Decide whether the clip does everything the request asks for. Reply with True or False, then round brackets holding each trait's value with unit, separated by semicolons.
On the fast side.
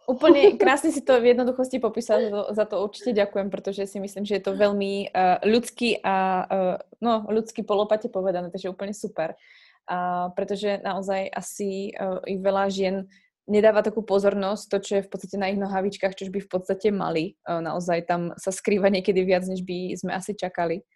True (180 wpm)